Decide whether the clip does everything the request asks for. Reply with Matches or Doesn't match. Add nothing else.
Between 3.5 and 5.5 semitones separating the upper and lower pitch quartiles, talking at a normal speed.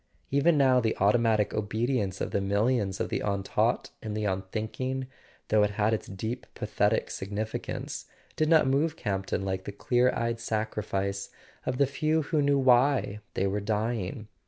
Matches